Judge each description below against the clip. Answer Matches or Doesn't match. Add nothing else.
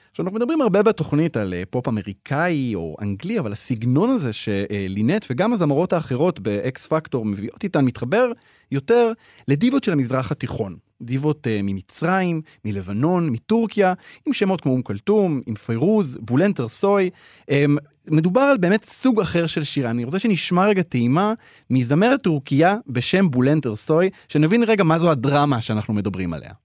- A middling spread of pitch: Doesn't match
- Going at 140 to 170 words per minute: Matches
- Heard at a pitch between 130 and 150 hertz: Matches